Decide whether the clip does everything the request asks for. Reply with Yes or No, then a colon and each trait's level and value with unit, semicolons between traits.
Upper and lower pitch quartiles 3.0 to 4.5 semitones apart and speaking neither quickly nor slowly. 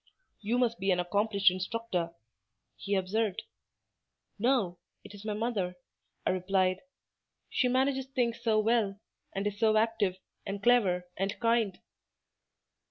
No: average, 3.4 semitones; slow, 130 wpm